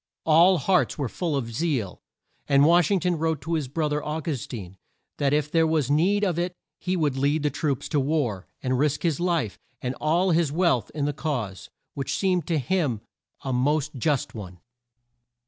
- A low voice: No, medium, 150 Hz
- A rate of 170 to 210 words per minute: Yes, average, 195 wpm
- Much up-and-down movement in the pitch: No, average, 4.1 semitones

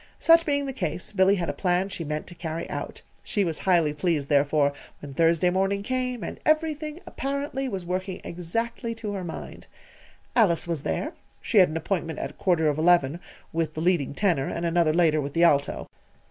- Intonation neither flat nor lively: Yes, average, 4.5 semitones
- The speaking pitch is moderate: Yes, medium, 175 Hz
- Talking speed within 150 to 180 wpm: No, average, 190 wpm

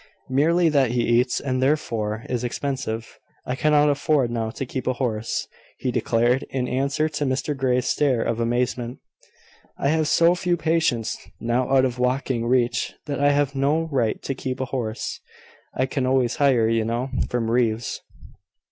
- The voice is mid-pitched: No, low, 130 Hz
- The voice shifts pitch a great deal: No, average, 3.0 semitones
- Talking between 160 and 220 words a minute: Yes, average, 170 wpm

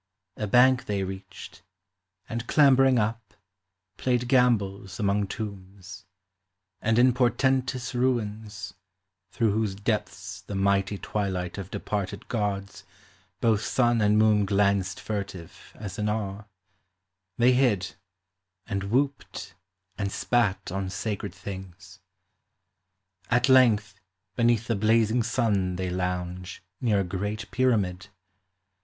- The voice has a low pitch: Yes, low, 105 Hz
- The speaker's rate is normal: No, slow, 110 wpm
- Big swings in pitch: No, average, 3.4 semitones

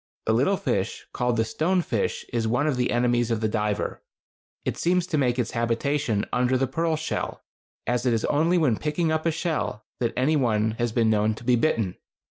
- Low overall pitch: Yes, low, 125 Hz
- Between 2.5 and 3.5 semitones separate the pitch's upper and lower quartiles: No, average, 5.2 semitones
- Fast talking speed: Yes, fast, 210 wpm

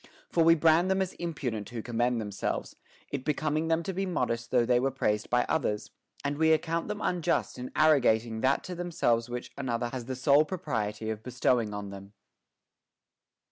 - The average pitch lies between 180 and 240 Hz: No, low, 130 Hz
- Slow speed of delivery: No, average, 180 wpm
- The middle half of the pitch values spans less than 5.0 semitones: No, wide, 5.6 semitones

